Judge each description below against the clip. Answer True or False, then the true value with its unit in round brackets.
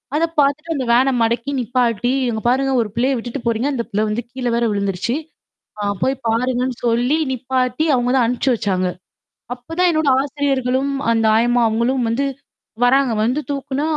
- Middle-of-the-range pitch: False (250 Hz)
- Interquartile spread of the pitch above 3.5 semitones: False (2.7 semitones)